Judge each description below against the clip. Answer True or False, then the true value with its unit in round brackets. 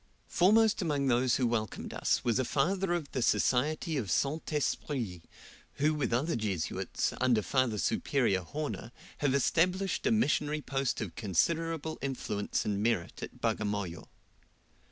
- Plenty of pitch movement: True (5.9 semitones)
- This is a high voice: False (135 Hz)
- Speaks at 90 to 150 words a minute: True (140 wpm)